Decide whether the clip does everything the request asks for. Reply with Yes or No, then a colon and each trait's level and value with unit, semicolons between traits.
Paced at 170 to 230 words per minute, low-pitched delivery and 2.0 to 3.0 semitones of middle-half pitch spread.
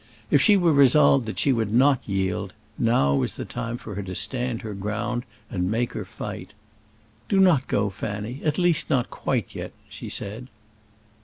No: average, 180 wpm; low, 115 Hz; average, 5.0 semitones